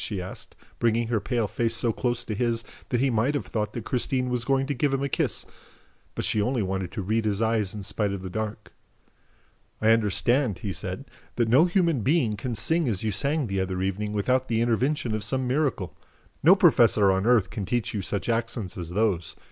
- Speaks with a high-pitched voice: No, low, 115 Hz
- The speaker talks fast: Yes, fast, 215 wpm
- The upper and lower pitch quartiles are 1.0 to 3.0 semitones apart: No, average, 3.7 semitones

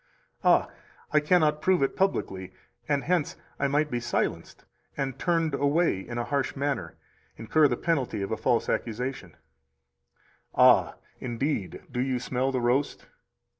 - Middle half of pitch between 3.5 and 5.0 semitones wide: Yes, average, 3.9 semitones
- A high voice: No, low, 135 Hz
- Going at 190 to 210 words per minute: No, average, 145 wpm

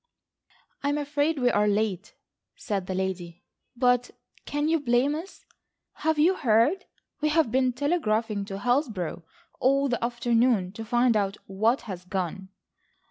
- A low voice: No, high, 240 Hz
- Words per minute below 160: Yes, average, 140 wpm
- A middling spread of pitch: No, wide, 5.9 semitones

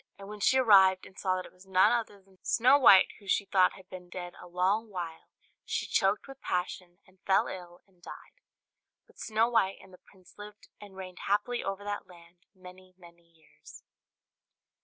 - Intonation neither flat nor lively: No, narrow, 2.1 semitones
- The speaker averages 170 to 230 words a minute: Yes, average, 195 wpm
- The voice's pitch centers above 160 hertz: Yes, high, 190 Hz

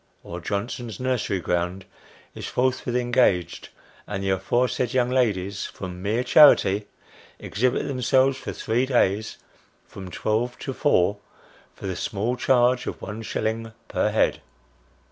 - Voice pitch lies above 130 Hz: No, low, 115 Hz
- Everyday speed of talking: No, slow, 130 wpm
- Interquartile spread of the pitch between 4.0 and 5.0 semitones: Yes, average, 4.5 semitones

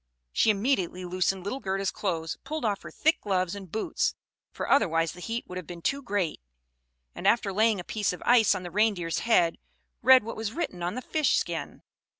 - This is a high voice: Yes, high, 200 Hz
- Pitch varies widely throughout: No, average, 4.2 semitones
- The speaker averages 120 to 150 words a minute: No, average, 200 wpm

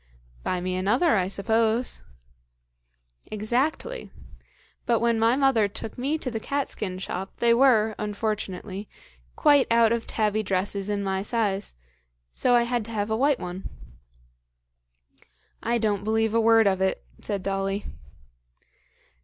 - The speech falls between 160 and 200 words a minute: No, average, 140 wpm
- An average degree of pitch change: Yes, average, 3.0 semitones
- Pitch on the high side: Yes, high, 220 Hz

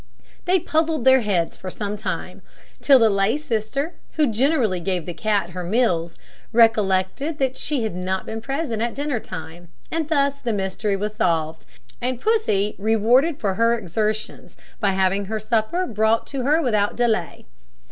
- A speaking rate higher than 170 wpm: No, average, 165 wpm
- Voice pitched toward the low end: No, high, 220 Hz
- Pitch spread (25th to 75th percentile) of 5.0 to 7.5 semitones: Yes, wide, 5.6 semitones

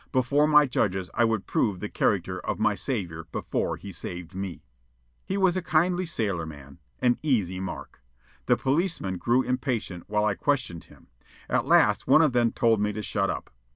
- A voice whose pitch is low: Yes, low, 110 Hz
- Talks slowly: No, average, 180 wpm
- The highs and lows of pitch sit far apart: Yes, wide, 6.6 semitones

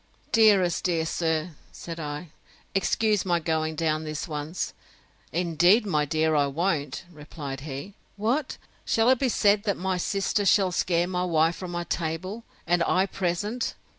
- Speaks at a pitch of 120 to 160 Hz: No, medium, 175 Hz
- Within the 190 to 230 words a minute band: No, average, 155 wpm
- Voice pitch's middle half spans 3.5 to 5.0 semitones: Yes, average, 3.8 semitones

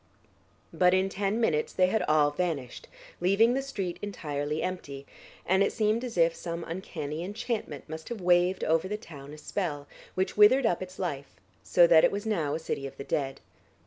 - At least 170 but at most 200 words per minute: Yes, average, 190 wpm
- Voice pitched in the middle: Yes, medium, 180 Hz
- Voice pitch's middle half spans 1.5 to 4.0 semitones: No, average, 4.7 semitones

